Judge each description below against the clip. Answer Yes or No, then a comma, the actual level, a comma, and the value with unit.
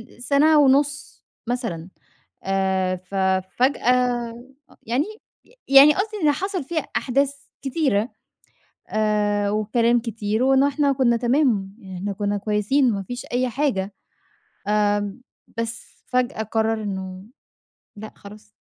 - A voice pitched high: Yes, high, 235 Hz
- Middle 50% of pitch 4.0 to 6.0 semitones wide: Yes, average, 4.7 semitones